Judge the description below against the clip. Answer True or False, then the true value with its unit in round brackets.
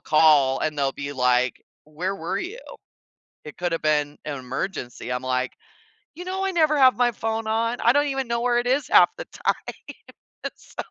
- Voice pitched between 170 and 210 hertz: True (185 Hz)